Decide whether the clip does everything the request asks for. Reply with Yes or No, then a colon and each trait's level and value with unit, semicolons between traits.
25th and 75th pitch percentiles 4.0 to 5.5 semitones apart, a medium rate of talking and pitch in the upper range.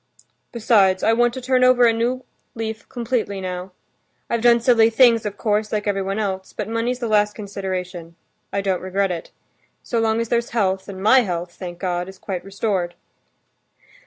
No: average, 3.5 semitones; average, 180 wpm; high, 210 Hz